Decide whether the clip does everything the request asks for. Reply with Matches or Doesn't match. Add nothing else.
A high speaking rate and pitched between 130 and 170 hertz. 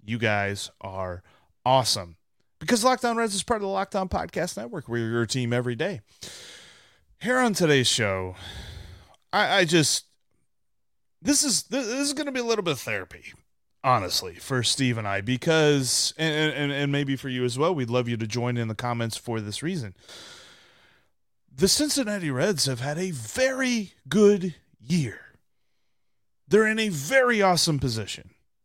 Doesn't match